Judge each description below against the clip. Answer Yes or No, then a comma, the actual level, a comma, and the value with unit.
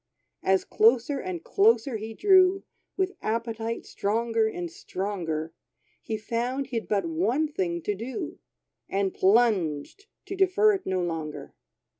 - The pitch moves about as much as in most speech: No, wide, 7.7 semitones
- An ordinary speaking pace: No, slow, 130 wpm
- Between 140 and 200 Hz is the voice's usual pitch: No, high, 225 Hz